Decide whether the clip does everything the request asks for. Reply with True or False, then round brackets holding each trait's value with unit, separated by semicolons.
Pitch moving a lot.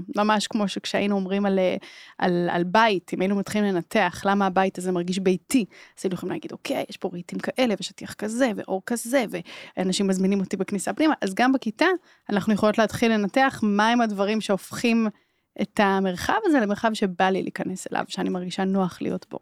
False (3.0 semitones)